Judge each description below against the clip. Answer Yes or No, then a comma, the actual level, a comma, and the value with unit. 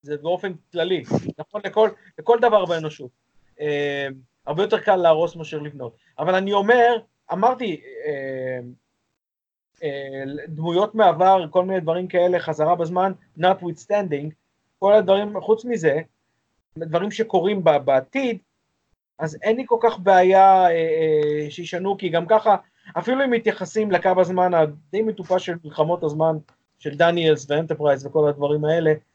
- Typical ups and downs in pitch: Yes, average, 4.7 semitones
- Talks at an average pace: Yes, average, 140 wpm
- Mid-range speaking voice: Yes, medium, 175 Hz